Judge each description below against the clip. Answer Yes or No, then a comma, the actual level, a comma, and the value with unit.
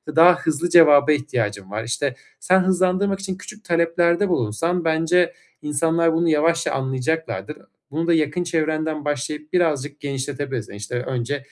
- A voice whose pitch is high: No, medium, 155 Hz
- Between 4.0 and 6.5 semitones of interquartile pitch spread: No, average, 3.4 semitones